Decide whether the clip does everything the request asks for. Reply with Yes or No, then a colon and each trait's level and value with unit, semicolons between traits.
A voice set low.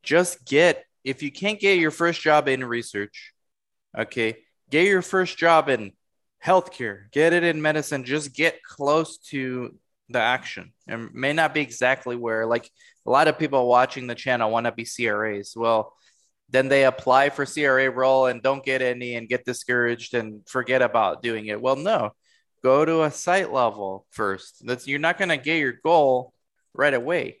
Yes: low, 130 Hz